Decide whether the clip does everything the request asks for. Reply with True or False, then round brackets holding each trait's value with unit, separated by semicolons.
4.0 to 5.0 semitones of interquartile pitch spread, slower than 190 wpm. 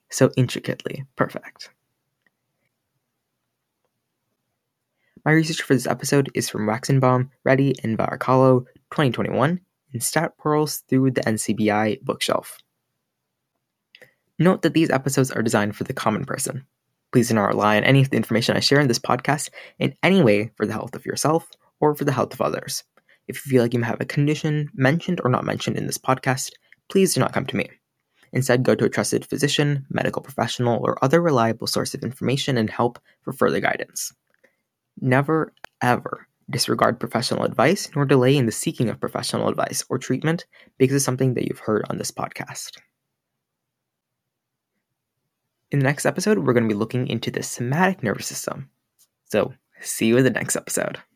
False (3.5 semitones; 170 wpm)